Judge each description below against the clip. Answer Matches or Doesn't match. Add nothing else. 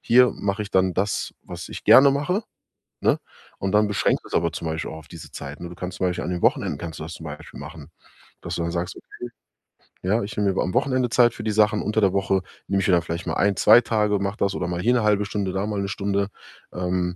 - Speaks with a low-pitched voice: Matches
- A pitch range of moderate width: Matches